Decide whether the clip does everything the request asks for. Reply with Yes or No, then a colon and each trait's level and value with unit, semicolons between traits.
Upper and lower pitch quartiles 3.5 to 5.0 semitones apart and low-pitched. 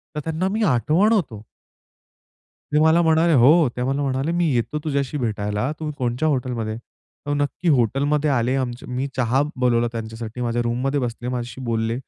Yes: average, 4.2 semitones; low, 130 Hz